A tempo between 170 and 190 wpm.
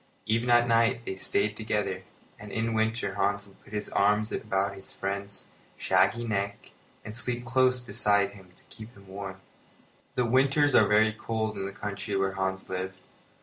Yes: average, 175 wpm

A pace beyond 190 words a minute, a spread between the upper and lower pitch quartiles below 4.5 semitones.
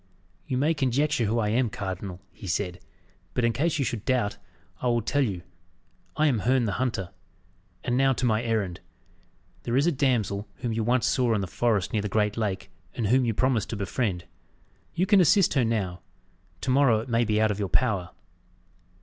Yes: average, 200 wpm; average, 4.0 semitones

